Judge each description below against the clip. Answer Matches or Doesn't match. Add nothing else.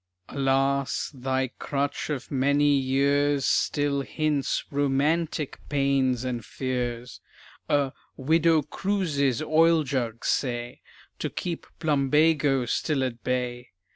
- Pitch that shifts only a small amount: Matches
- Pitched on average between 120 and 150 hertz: Matches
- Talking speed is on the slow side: Matches